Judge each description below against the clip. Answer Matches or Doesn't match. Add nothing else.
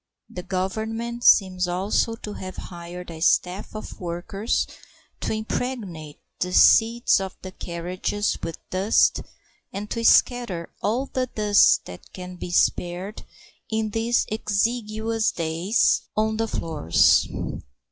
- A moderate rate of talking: Doesn't match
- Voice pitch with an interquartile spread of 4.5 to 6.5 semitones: Doesn't match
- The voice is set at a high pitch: Matches